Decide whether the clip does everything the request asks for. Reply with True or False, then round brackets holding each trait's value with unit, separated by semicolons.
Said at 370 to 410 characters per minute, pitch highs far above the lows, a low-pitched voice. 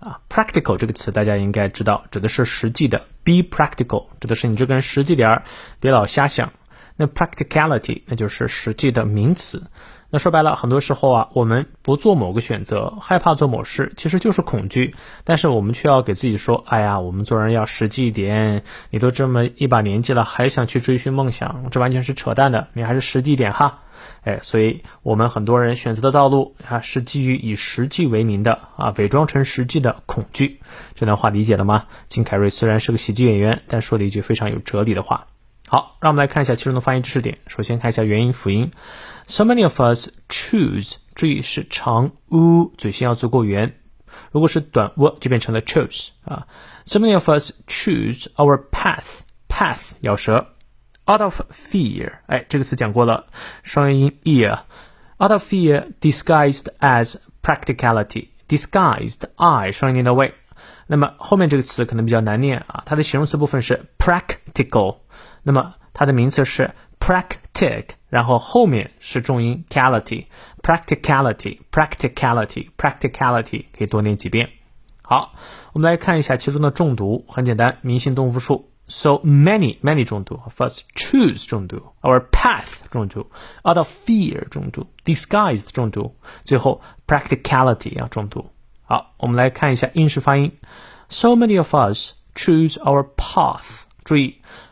False (390 characters per minute; 4.5 semitones; 130 Hz)